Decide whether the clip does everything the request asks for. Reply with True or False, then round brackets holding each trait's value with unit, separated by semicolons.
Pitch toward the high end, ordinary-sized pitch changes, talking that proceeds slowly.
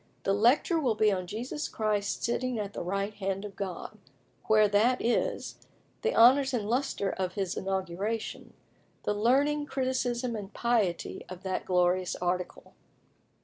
False (210 Hz; 4.1 semitones; 145 wpm)